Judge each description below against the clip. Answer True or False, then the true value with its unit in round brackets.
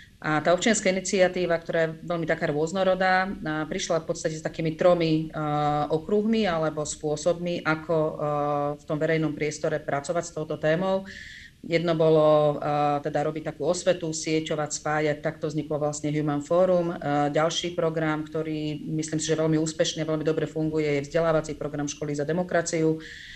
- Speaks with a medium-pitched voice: True (155 Hz)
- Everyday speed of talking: True (145 wpm)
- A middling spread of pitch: False (2.0 semitones)